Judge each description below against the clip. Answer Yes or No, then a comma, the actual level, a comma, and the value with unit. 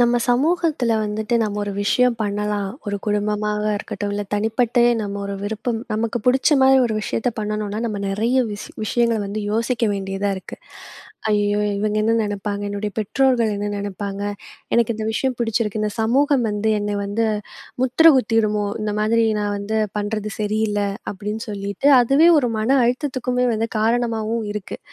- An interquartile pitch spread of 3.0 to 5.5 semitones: No, narrow, 2.5 semitones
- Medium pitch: No, high, 215 Hz